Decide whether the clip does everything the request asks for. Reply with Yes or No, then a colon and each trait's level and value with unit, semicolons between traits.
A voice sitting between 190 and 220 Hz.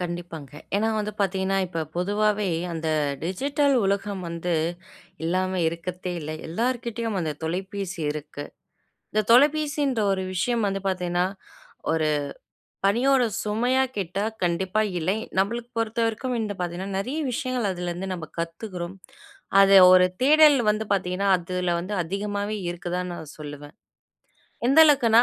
Yes: high, 195 Hz